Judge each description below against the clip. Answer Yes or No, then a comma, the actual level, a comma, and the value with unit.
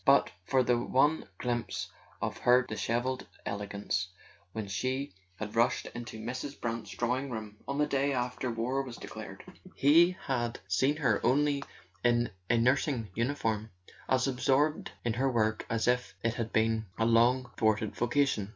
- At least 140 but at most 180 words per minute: Yes, average, 155 wpm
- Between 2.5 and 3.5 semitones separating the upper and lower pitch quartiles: Yes, average, 2.9 semitones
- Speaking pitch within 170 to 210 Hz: No, low, 120 Hz